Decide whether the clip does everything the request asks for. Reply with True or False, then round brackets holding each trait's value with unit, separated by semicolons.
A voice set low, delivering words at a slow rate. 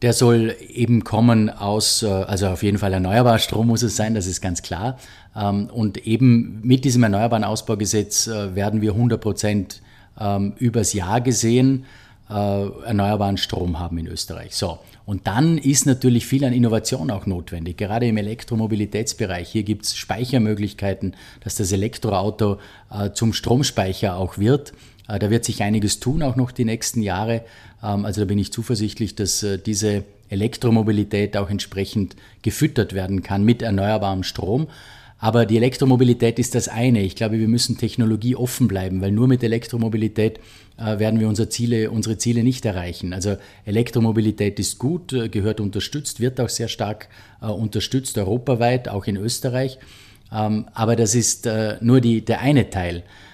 False (110 Hz; 150 wpm)